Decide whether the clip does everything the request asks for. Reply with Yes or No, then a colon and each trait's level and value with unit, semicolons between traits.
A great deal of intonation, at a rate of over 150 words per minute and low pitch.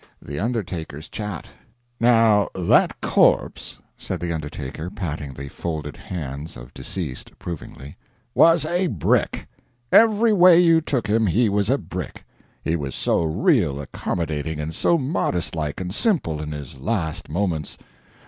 No: wide, 7.2 semitones; average, 140 wpm; very low, 85 Hz